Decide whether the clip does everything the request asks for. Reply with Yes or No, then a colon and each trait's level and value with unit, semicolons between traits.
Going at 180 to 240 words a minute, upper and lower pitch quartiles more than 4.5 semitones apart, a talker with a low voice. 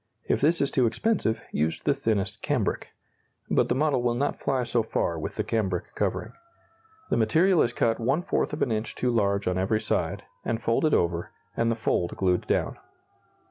Yes: average, 190 wpm; average, 5.3 semitones; low, 115 Hz